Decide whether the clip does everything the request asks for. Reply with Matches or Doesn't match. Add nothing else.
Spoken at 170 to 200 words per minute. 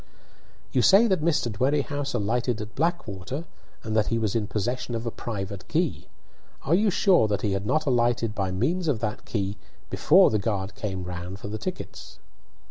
Matches